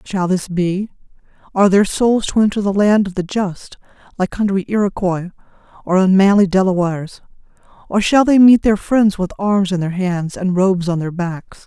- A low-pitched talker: No, high, 190 Hz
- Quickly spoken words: No, average, 180 wpm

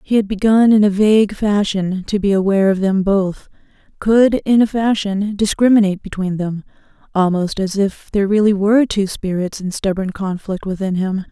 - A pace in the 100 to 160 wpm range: No, average, 175 wpm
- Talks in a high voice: Yes, high, 200 Hz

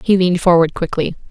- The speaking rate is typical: Yes, average, 185 wpm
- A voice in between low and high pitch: Yes, medium, 175 Hz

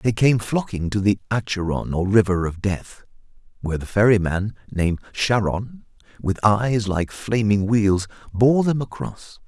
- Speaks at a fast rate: No, average, 145 wpm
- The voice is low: Yes, low, 105 Hz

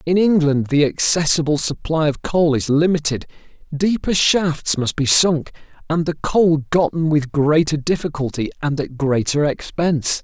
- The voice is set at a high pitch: No, medium, 155 Hz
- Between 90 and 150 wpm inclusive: Yes, average, 145 wpm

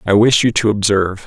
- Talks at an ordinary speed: No, fast, 240 wpm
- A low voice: Yes, low, 105 Hz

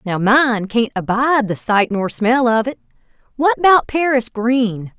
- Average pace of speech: Yes, average, 170 wpm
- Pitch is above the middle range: Yes, high, 235 Hz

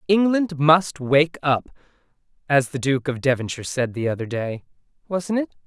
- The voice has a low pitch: No, medium, 150 Hz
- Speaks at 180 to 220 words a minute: No, average, 160 wpm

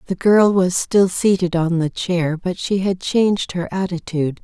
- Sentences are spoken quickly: No, average, 190 wpm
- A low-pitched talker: No, medium, 180 Hz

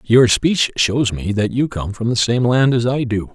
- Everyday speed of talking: No, fast, 250 wpm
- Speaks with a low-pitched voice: Yes, low, 120 Hz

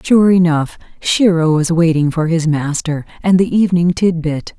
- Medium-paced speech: Yes, average, 170 wpm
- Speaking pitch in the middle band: Yes, medium, 170 Hz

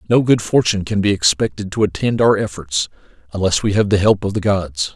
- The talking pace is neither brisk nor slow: No, fast, 220 wpm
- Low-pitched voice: Yes, low, 100 Hz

